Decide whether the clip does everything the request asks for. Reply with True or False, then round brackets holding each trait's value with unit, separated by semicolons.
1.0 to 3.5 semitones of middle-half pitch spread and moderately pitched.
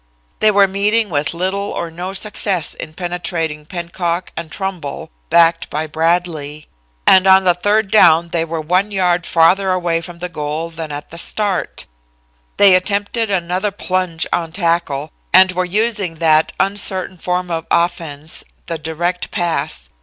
True (2.6 semitones; 175 Hz)